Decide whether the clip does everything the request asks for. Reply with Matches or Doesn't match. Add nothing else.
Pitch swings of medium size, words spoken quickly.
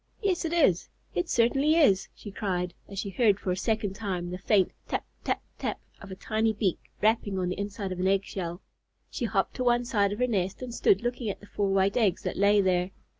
Matches